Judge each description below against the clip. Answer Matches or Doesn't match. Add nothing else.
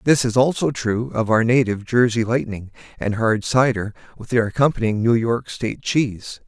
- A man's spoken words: Matches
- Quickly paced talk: Doesn't match